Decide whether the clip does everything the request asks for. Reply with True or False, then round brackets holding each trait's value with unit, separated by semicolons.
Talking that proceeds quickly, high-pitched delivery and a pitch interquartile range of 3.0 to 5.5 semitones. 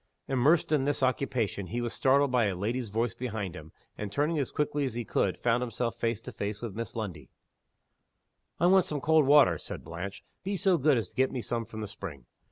False (220 wpm; 120 Hz; 5.0 semitones)